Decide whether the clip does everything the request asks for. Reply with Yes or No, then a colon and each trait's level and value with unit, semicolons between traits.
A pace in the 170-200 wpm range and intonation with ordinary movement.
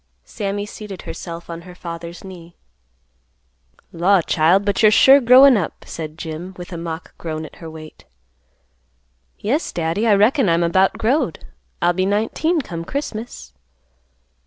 No: average, 145 wpm; average, 4.3 semitones